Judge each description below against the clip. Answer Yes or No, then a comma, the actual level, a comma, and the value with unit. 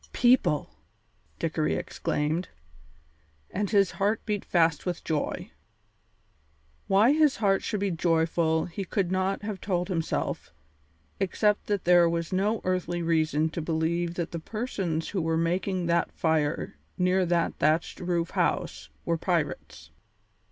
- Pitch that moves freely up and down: No, average, 3.0 semitones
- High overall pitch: No, medium, 175 Hz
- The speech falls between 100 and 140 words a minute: Yes, slow, 135 wpm